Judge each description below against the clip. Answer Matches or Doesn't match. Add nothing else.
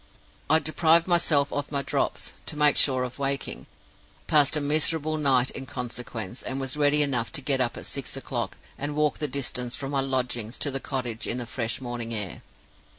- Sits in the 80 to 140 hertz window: Matches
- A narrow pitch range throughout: Doesn't match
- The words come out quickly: Doesn't match